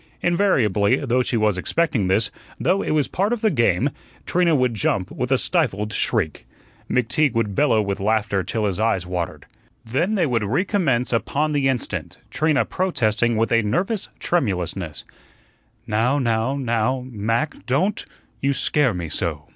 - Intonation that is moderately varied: No, wide, 6.0 semitones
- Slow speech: No, average, 155 wpm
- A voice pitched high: No, low, 120 Hz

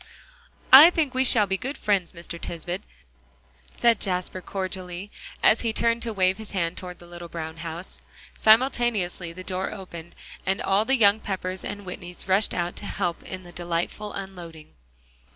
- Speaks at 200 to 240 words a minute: No, average, 170 wpm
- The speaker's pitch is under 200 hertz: Yes, medium, 185 Hz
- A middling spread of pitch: Yes, average, 3.3 semitones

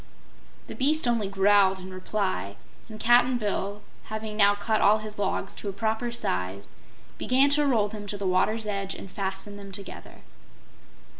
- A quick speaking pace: No, average, 165 wpm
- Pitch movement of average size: No, narrow, 2.2 semitones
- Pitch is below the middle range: No, high, 205 Hz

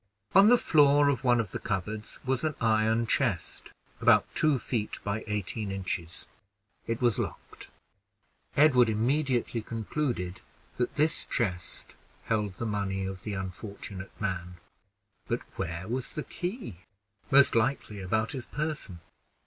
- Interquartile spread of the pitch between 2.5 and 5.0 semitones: No, wide, 5.4 semitones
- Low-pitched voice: Yes, low, 110 Hz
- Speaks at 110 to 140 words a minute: Yes, slow, 135 wpm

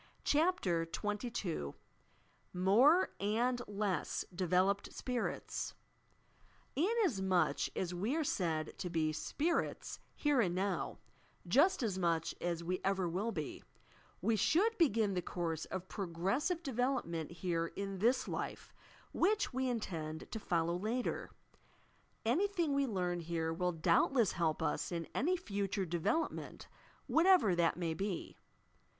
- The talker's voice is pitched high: Yes, high, 195 Hz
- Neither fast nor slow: No, slow, 130 wpm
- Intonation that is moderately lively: No, wide, 6.7 semitones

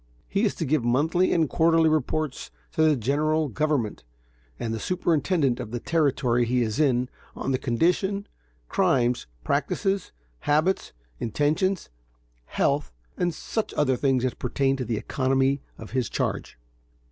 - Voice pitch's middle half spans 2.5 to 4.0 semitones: No, average, 4.5 semitones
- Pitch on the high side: No, medium, 140 Hz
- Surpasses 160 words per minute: No, average, 145 wpm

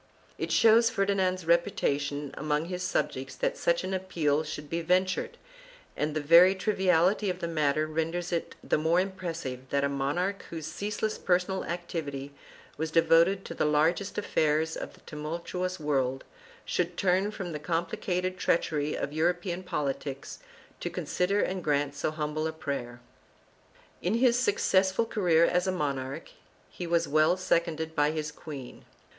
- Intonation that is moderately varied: Yes, average, 3.5 semitones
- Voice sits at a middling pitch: Yes, medium, 165 Hz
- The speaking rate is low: No, average, 155 wpm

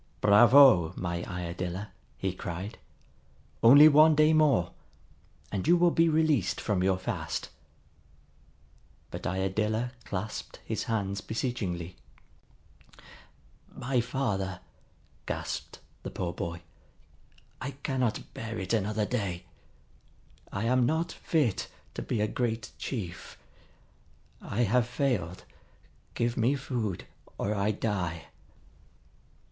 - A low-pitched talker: Yes, low, 110 Hz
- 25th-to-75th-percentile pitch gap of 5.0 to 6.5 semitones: Yes, wide, 5.4 semitones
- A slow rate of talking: Yes, slow, 110 wpm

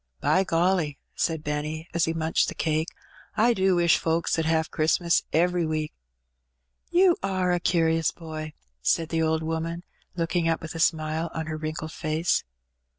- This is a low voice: No, medium, 165 Hz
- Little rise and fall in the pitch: Yes, narrow, 1.6 semitones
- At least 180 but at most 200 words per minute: No, average, 170 wpm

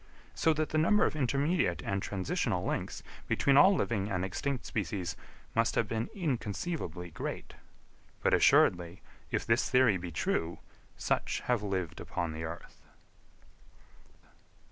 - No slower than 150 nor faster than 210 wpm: No, slow, 135 wpm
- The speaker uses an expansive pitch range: Yes, wide, 7.8 semitones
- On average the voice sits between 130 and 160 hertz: No, low, 105 Hz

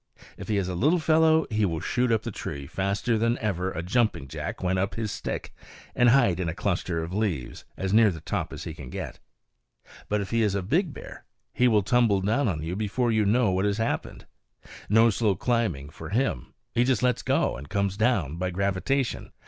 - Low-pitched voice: Yes, low, 100 Hz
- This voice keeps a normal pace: No, fast, 215 wpm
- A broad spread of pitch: No, average, 4.4 semitones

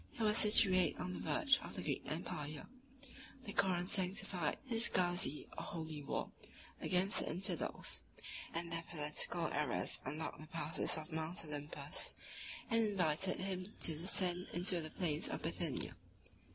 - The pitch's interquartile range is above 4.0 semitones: No, average, 3.5 semitones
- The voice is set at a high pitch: No, medium, 175 Hz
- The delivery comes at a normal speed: Yes, average, 150 wpm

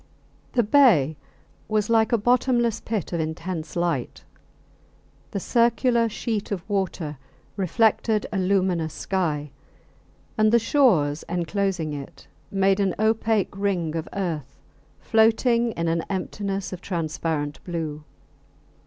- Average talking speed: No, slow, 120 wpm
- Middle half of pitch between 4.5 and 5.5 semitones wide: Yes, average, 5.2 semitones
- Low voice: No, high, 195 Hz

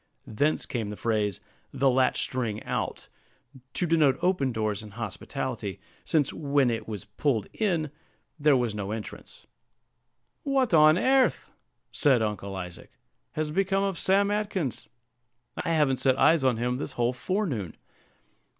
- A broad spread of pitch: Yes, wide, 6.8 semitones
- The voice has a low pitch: Yes, low, 130 Hz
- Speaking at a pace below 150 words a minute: Yes, average, 140 wpm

